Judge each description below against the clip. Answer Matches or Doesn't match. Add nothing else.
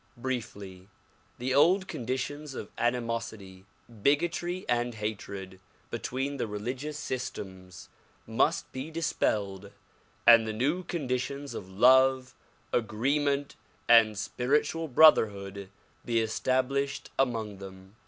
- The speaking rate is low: Matches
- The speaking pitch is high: Doesn't match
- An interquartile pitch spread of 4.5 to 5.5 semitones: Matches